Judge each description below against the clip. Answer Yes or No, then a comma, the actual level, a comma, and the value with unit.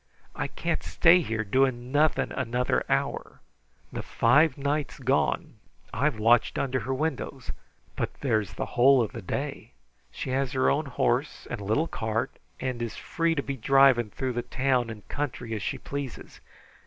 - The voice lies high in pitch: No, low, 130 Hz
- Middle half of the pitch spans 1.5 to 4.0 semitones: Yes, average, 3.2 semitones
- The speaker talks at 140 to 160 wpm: Yes, average, 155 wpm